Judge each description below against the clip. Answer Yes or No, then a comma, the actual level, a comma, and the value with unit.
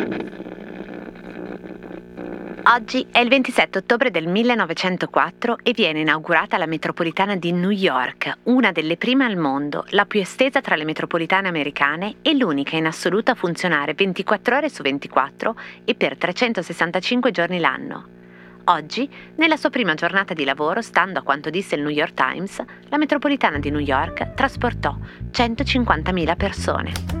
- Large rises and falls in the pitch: Yes, wide, 7.8 semitones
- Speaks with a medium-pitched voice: Yes, medium, 175 Hz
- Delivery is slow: No, average, 145 wpm